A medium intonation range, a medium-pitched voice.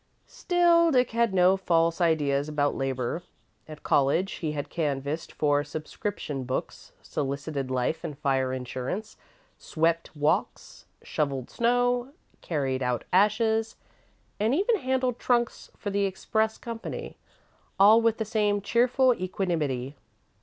No: wide, 7.9 semitones; medium, 175 Hz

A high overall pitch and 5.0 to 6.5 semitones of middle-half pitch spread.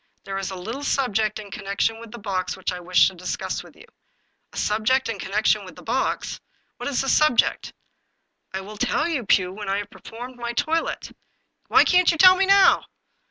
Yes: high, 220 Hz; wide, 5.4 semitones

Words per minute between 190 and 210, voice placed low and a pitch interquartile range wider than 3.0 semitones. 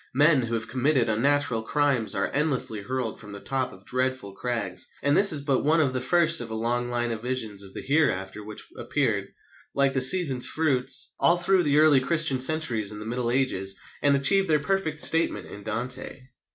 Yes: average, 200 wpm; low, 130 Hz; average, 4.5 semitones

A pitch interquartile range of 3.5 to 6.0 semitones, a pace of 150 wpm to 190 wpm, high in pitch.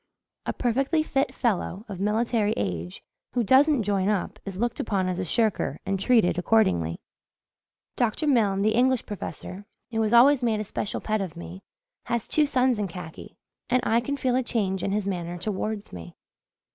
Yes: average, 4.2 semitones; average, 180 wpm; high, 215 Hz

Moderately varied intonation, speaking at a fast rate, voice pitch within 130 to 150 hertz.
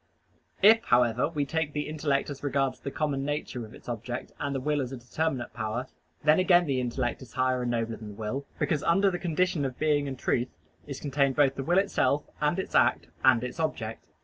Yes: average, 3.6 semitones; fast, 220 wpm; medium, 140 Hz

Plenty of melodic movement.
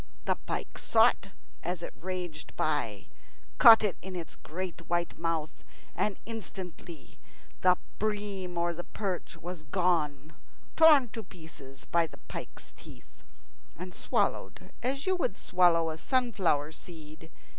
No: average, 3.4 semitones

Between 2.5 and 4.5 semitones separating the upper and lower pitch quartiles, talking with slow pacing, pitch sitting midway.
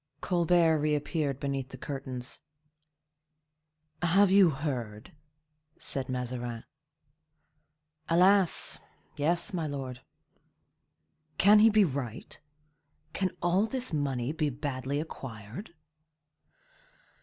No: average, 5.3 semitones; slow, 85 wpm; medium, 145 Hz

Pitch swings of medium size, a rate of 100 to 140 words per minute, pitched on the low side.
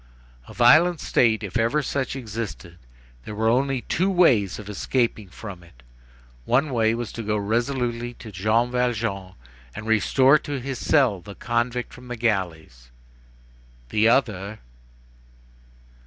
Yes: average, 3.4 semitones; slow, 135 wpm; low, 115 Hz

